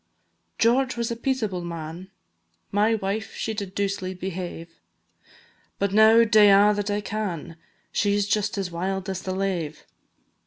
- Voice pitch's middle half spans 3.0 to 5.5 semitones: No, narrow, 2.6 semitones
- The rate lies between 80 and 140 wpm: No, average, 150 wpm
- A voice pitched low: No, high, 200 Hz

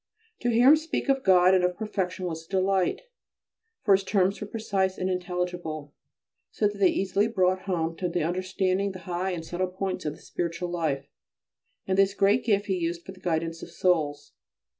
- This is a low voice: No, medium, 185 Hz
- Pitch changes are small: Yes, narrow, 2.1 semitones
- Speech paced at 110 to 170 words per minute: No, average, 195 wpm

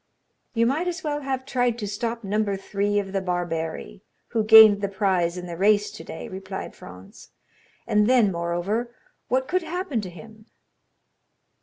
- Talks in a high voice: Yes, high, 210 Hz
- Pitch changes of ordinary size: Yes, average, 4.1 semitones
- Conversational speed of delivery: Yes, average, 160 wpm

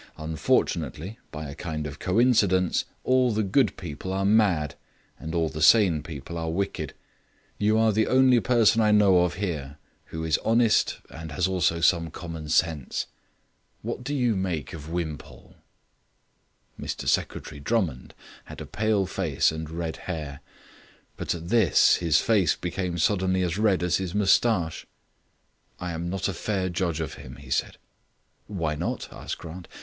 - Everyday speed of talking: Yes, average, 160 wpm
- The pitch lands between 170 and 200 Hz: No, very low, 90 Hz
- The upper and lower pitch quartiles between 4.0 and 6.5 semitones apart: Yes, average, 4.5 semitones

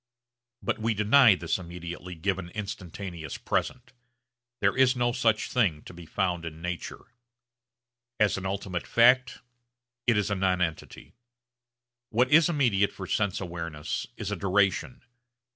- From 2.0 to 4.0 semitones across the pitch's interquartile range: No, average, 4.5 semitones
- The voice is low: Yes, low, 100 Hz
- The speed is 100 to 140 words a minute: Yes, slow, 135 wpm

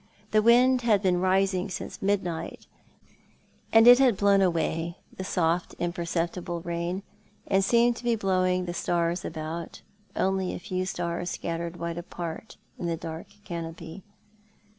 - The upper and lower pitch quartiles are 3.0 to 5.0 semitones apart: No, narrow, 2.5 semitones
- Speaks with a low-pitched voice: No, medium, 180 Hz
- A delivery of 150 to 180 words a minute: No, average, 140 wpm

